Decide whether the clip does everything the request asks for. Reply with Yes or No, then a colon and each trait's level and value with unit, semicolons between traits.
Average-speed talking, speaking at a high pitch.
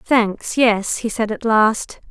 Yes: average, 170 wpm; high, 220 Hz